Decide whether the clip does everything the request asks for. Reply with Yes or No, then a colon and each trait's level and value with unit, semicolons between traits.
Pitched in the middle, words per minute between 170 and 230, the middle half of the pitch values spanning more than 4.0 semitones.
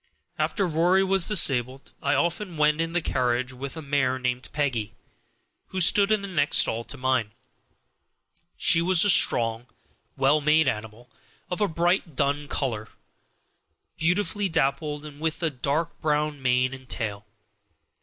No: medium, 145 Hz; average, 150 wpm; average, 4.8 semitones